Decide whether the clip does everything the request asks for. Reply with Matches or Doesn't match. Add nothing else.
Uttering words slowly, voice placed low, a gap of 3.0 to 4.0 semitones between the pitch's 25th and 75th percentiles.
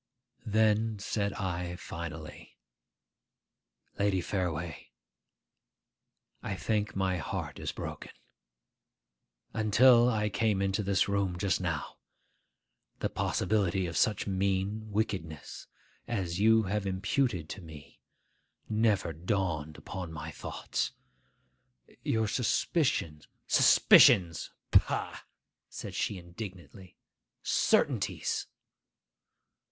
Matches